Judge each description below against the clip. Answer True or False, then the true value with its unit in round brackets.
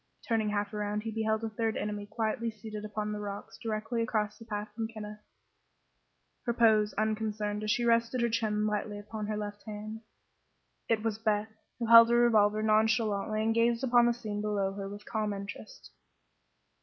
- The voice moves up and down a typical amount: False (1.4 semitones)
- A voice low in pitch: False (215 Hz)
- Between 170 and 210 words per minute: True (180 wpm)